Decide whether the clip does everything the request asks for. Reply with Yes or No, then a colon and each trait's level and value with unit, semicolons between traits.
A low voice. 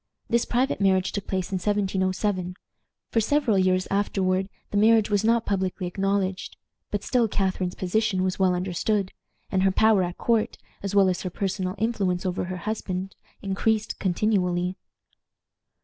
No: high, 195 Hz